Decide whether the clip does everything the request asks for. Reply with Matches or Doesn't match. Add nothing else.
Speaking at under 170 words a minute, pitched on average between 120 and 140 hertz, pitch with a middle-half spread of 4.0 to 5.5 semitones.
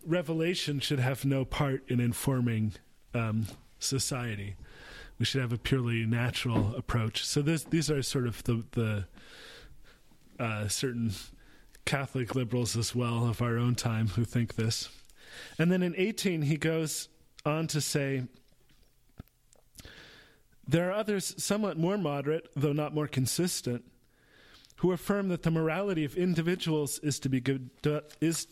Matches